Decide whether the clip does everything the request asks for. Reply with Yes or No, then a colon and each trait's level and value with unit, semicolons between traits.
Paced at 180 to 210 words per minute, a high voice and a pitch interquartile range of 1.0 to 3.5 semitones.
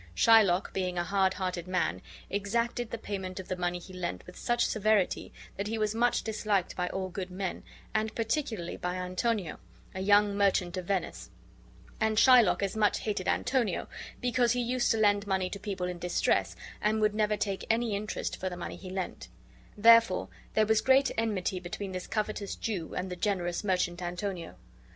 Yes: average, 185 wpm; high, 200 Hz; average, 3.1 semitones